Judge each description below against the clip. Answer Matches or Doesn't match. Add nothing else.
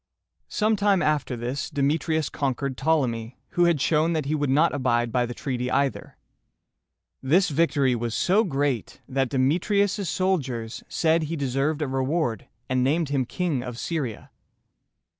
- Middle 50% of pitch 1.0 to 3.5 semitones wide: Doesn't match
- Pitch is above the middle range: Doesn't match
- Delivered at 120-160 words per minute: Matches